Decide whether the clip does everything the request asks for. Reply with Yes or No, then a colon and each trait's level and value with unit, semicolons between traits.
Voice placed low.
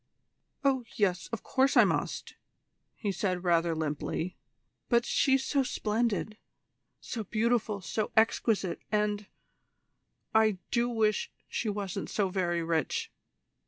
No: high, 210 Hz